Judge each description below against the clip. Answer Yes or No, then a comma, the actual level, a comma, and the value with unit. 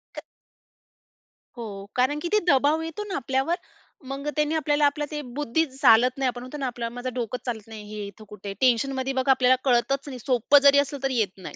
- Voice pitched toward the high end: Yes, very high, 260 Hz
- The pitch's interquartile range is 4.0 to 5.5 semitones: No, average, 3.3 semitones